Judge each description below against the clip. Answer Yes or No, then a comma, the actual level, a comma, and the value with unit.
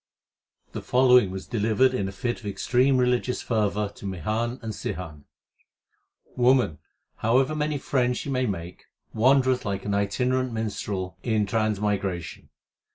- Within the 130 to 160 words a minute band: Yes, average, 140 wpm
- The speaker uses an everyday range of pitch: Yes, average, 4.1 semitones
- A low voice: Yes, low, 110 Hz